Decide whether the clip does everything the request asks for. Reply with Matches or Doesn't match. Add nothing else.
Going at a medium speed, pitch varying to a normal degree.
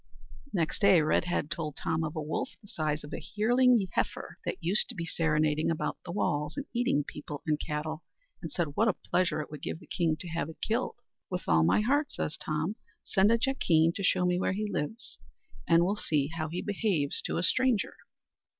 Doesn't match